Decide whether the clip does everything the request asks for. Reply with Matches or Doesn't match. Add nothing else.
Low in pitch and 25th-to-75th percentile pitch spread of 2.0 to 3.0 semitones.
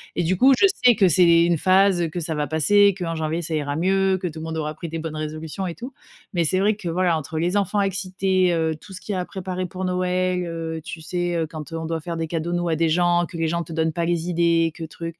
Doesn't match